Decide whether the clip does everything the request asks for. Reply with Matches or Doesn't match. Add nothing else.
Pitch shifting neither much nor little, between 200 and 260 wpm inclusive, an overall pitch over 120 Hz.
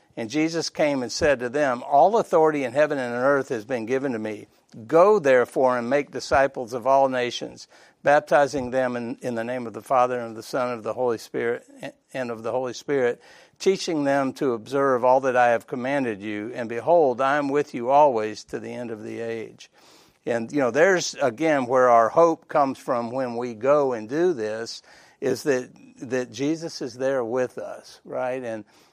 Matches